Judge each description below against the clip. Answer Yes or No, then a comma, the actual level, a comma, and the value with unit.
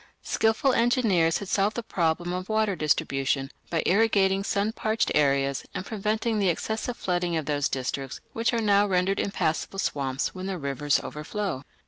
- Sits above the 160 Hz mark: Yes, high, 190 Hz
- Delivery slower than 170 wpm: Yes, average, 160 wpm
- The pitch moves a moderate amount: No, wide, 6.0 semitones